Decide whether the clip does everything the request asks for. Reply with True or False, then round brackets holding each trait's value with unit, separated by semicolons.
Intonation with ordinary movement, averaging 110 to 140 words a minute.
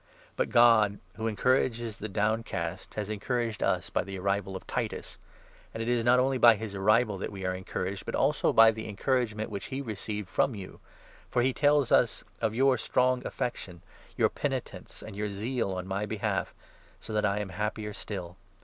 False (3.3 semitones; 195 wpm)